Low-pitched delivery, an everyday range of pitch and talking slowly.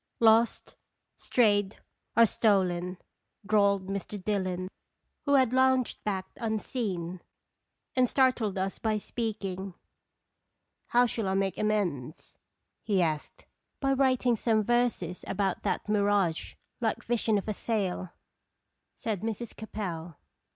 No: high, 210 Hz; average, 3.5 semitones; slow, 120 wpm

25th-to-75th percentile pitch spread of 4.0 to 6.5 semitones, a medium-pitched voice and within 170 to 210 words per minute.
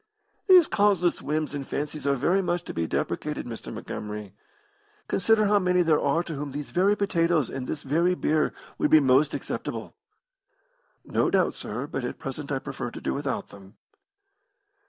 Yes: average, 4.9 semitones; medium, 150 Hz; average, 175 wpm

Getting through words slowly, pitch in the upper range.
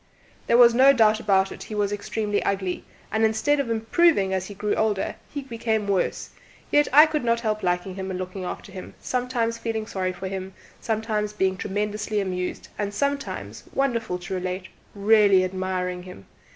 No: average, 180 wpm; high, 210 Hz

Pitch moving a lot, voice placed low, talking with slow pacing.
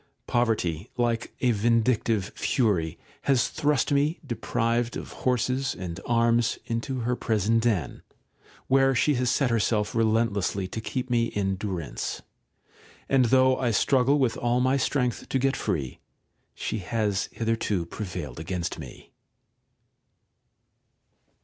No: average, 3.8 semitones; low, 115 Hz; slow, 125 wpm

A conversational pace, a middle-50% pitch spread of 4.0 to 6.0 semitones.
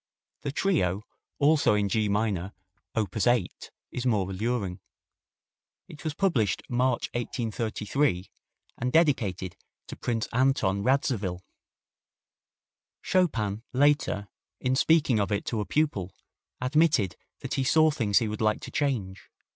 No: slow, 125 wpm; wide, 5.6 semitones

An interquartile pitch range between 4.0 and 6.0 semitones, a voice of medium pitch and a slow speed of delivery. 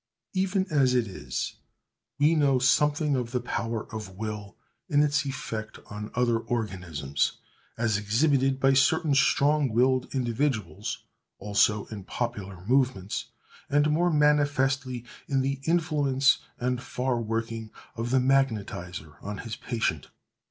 No: average, 4.4 semitones; low, 125 Hz; slow, 130 wpm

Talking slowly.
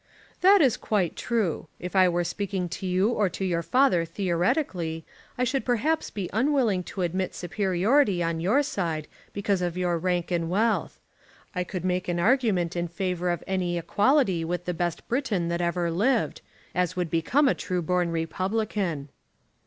No: average, 170 wpm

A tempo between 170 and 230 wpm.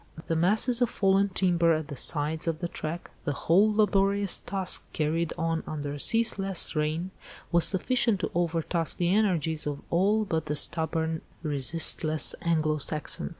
No: average, 155 wpm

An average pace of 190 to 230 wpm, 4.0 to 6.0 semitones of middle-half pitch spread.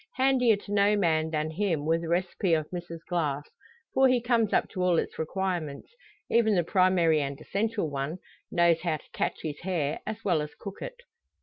Yes: average, 195 wpm; average, 4.6 semitones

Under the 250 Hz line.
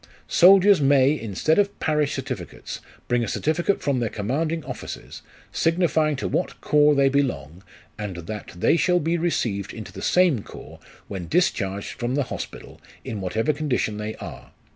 Yes: medium, 140 Hz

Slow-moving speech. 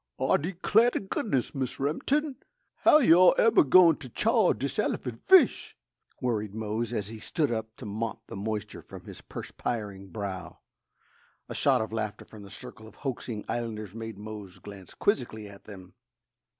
No: average, 165 wpm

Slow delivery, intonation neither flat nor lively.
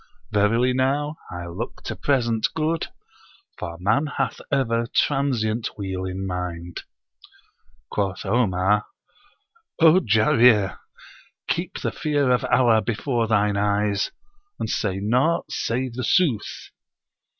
Yes: slow, 115 wpm; average, 4.5 semitones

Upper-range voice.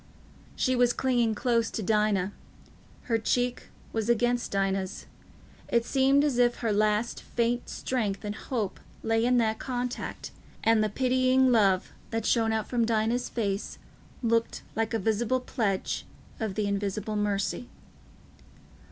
Yes: high, 225 Hz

